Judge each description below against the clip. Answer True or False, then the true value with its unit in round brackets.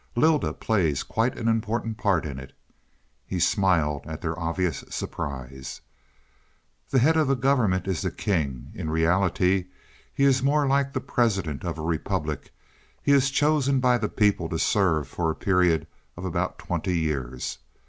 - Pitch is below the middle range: True (95 Hz)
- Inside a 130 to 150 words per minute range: False (160 wpm)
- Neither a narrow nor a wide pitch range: False (7.5 semitones)